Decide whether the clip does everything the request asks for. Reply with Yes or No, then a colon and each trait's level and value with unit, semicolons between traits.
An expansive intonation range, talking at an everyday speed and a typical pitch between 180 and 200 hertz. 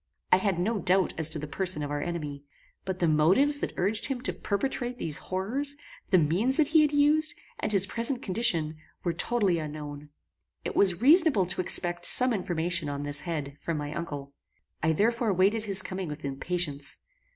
Yes: wide, 6.8 semitones; average, 185 wpm; medium, 185 Hz